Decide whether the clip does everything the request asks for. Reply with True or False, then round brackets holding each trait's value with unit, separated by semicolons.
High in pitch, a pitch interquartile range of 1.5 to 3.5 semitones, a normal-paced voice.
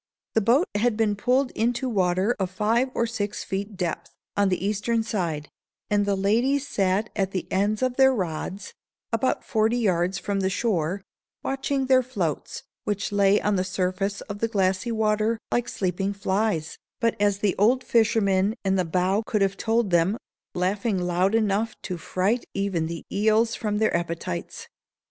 True (205 Hz; 3.1 semitones; 170 wpm)